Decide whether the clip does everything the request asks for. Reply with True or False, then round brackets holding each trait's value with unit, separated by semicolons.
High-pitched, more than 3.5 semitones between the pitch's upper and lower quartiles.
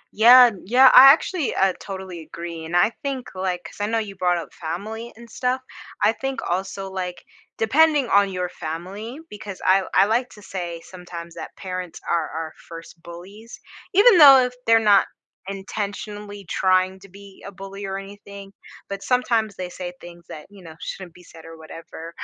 True (195 Hz; 3.9 semitones)